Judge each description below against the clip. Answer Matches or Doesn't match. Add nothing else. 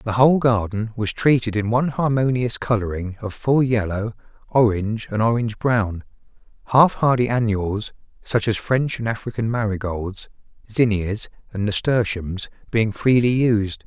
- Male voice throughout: Matches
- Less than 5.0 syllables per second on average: Matches